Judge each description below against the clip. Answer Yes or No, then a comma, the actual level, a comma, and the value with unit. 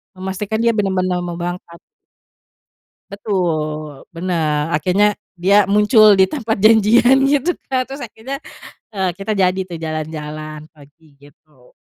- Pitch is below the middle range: No, medium, 185 Hz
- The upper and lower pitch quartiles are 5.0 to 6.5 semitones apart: Yes, wide, 5.4 semitones